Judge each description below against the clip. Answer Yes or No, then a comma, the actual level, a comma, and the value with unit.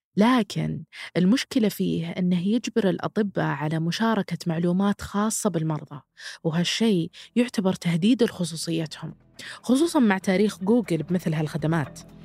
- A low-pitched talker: No, medium, 185 Hz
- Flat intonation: No, average, 4.7 semitones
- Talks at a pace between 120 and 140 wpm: No, average, 105 wpm